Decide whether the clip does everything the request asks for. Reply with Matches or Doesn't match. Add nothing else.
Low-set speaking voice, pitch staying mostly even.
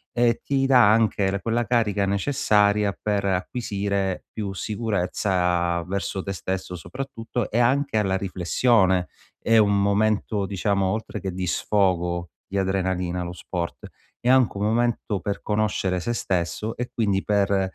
Doesn't match